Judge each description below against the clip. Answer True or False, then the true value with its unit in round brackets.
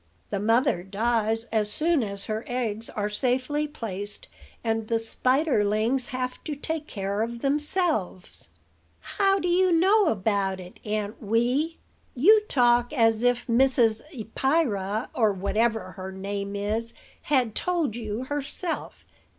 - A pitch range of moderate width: True (5.0 semitones)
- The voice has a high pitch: True (230 Hz)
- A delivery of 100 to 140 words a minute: True (135 wpm)